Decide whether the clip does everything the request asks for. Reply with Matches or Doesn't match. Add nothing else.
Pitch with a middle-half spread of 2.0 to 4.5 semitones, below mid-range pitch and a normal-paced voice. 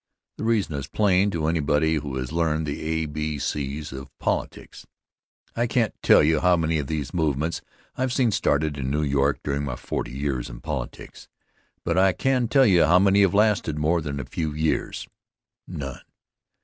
Matches